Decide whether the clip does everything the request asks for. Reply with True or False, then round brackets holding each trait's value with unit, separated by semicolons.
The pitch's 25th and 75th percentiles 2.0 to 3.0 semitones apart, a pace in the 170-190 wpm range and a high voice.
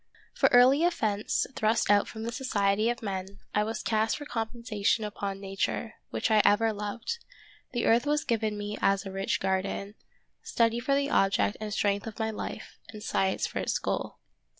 True (2.6 semitones; 180 wpm; 215 Hz)